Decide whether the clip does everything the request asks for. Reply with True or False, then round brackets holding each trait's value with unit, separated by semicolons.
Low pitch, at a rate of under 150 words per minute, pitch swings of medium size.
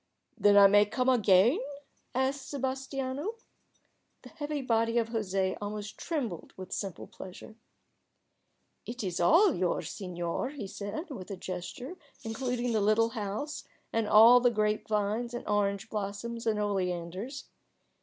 False (220 Hz; 140 wpm; 4.2 semitones)